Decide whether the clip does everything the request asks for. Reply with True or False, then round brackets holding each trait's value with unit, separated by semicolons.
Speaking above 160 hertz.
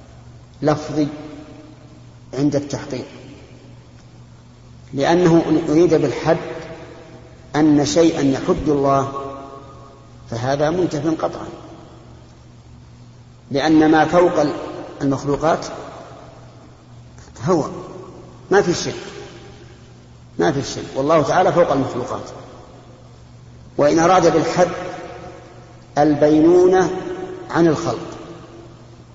False (150 Hz)